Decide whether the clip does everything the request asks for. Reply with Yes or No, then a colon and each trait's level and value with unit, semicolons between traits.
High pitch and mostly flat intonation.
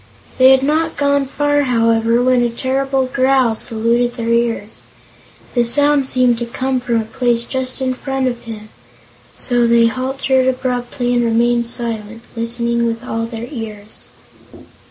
Yes: high, 240 Hz; narrow, 2.2 semitones